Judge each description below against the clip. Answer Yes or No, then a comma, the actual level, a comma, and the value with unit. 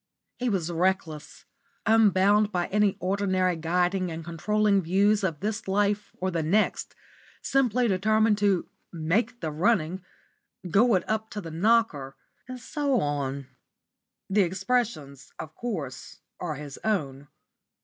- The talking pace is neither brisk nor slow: No, slow, 130 wpm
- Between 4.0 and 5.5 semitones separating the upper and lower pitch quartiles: Yes, average, 4.6 semitones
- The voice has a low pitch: No, high, 190 Hz